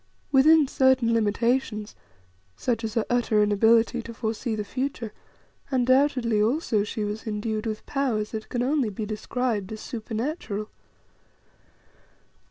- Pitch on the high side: Yes, high, 230 Hz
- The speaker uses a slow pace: Yes, slow, 125 wpm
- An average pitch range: Yes, average, 3.1 semitones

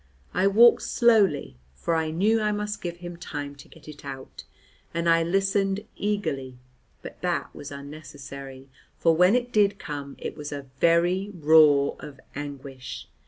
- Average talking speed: Yes, average, 160 wpm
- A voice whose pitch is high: No, medium, 165 Hz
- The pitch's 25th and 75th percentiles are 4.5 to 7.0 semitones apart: Yes, wide, 5.6 semitones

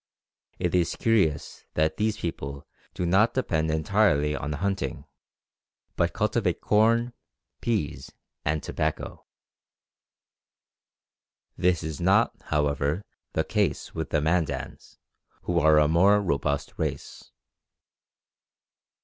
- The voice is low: Yes, very low, 80 Hz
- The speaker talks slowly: Yes, slow, 105 wpm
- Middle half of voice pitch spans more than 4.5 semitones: Yes, average, 5.0 semitones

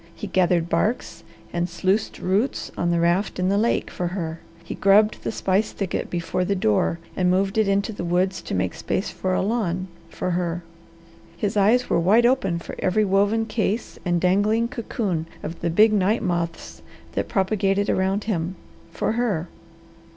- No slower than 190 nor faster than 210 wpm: No, average, 175 wpm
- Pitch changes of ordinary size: Yes, average, 3.4 semitones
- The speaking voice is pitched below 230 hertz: Yes, high, 190 Hz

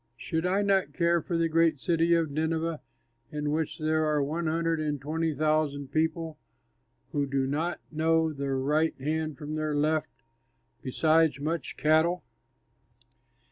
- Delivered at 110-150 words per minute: Yes, average, 140 wpm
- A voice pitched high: No, medium, 155 Hz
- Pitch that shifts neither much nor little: No, narrow, 1.7 semitones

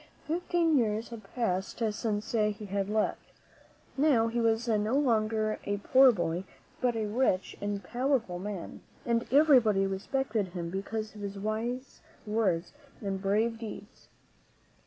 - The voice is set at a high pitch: Yes, high, 215 Hz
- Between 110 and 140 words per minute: Yes, slow, 135 wpm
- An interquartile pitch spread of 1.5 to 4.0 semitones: Yes, average, 3.0 semitones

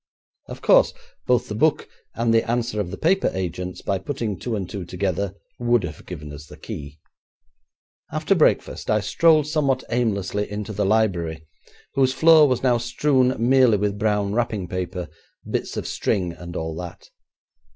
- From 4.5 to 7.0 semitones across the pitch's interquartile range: Yes, average, 5.1 semitones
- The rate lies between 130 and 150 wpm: No, average, 165 wpm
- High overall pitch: No, low, 105 Hz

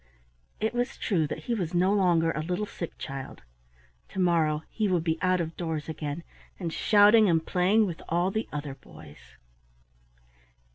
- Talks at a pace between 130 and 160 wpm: No, average, 170 wpm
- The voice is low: No, medium, 175 Hz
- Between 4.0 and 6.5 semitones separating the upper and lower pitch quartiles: No, average, 3.6 semitones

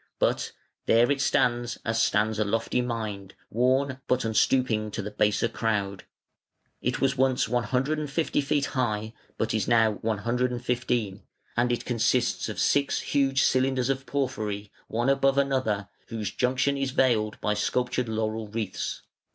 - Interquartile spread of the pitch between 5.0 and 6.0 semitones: No, average, 3.4 semitones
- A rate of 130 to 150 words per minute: Yes, average, 145 wpm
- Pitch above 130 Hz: No, low, 120 Hz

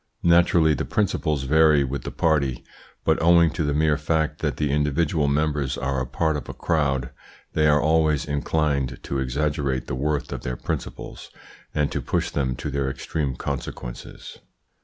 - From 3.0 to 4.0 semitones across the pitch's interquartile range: No, narrow, 2.5 semitones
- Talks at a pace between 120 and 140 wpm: No, average, 170 wpm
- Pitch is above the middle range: No, very low, 75 Hz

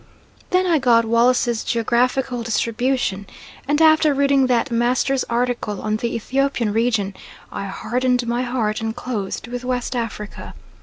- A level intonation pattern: Yes, narrow, 2.0 semitones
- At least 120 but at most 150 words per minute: Yes, average, 140 wpm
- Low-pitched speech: No, high, 245 Hz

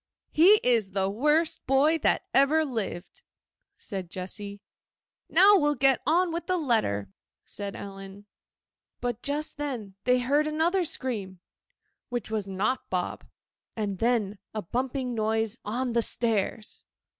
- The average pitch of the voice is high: Yes, high, 240 Hz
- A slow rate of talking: Yes, slow, 125 wpm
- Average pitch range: No, wide, 6.5 semitones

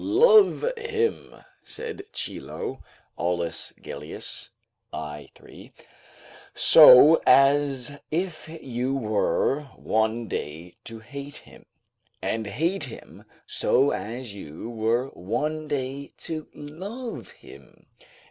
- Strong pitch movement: Yes, wide, 6.1 semitones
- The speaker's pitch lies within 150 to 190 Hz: No, low, 135 Hz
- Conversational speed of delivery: No, slow, 100 wpm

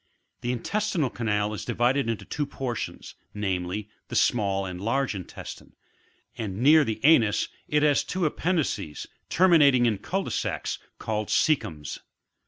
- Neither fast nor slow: Yes, average, 150 wpm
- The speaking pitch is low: Yes, low, 120 Hz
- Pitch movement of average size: No, wide, 6.2 semitones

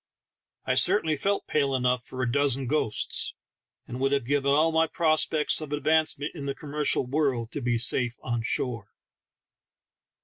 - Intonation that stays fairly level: No, average, 3.5 semitones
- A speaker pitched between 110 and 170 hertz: Yes, medium, 140 Hz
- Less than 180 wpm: Yes, average, 160 wpm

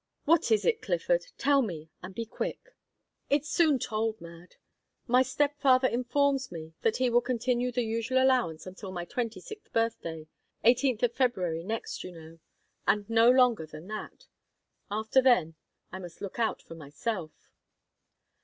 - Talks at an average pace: Yes, average, 160 wpm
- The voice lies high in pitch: Yes, high, 230 Hz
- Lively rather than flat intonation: Yes, wide, 6.0 semitones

